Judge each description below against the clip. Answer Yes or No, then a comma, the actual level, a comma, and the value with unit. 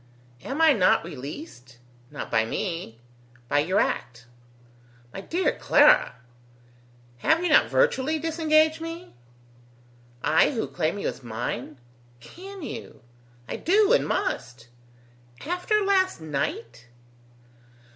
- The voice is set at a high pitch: Yes, high, 235 Hz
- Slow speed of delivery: Yes, slow, 115 wpm